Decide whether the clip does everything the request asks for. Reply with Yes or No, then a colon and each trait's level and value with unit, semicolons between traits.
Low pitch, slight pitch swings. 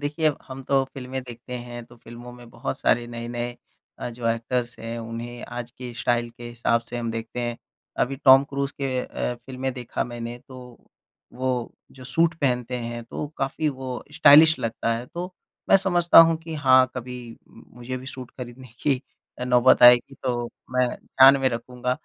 Yes: low, 125 Hz; narrow, 1.9 semitones